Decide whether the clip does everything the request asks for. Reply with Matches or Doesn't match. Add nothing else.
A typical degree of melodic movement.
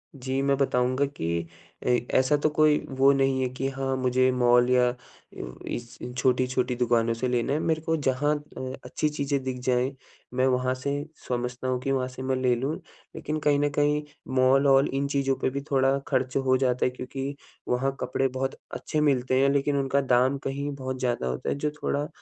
Doesn't match